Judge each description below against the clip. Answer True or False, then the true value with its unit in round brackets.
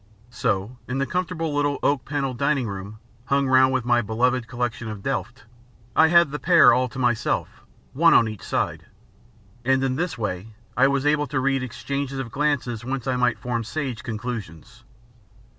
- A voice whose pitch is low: True (130 Hz)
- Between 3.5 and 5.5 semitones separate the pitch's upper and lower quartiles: False (2.8 semitones)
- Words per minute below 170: False (175 wpm)